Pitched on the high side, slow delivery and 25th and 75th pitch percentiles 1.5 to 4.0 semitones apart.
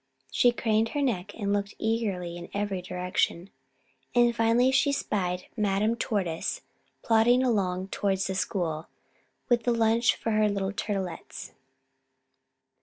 Yes: high, 205 Hz; slow, 130 wpm; average, 3.5 semitones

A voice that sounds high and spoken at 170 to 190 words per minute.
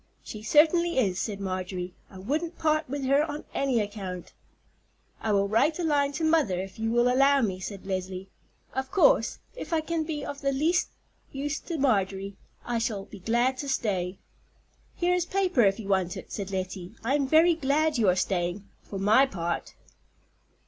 Yes: high, 240 Hz; average, 185 wpm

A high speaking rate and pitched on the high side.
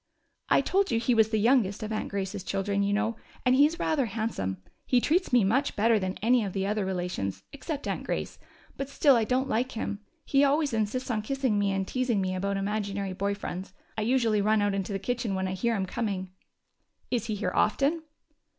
Yes: fast, 215 wpm; high, 215 Hz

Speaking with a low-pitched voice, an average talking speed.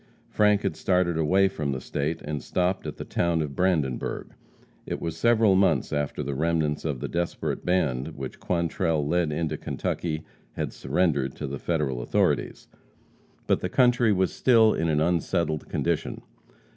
Yes: very low, 80 Hz; average, 160 wpm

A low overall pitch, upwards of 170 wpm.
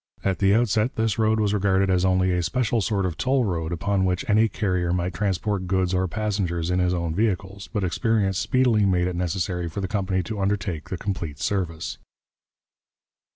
Yes: very low, 95 Hz; average, 190 wpm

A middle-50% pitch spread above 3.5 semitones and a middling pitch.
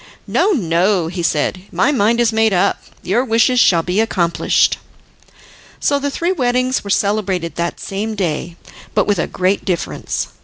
No: average, 5.1 semitones; high, 200 Hz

